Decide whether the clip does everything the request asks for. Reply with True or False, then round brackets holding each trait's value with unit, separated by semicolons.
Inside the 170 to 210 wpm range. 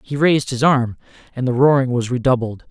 True (200 wpm)